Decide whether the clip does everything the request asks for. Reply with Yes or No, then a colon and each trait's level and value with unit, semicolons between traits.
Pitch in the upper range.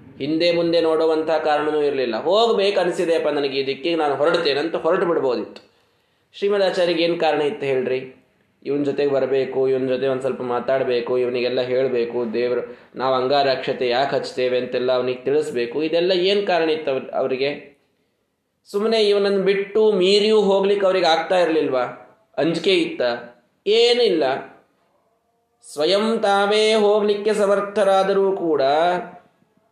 No: medium, 160 Hz